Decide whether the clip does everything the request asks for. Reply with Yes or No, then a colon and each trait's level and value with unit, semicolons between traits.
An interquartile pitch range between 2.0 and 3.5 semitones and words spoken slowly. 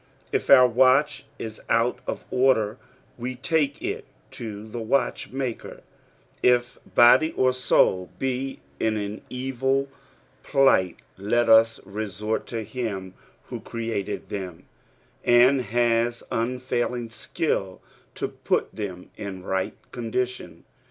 Yes: average, 3.1 semitones; slow, 115 wpm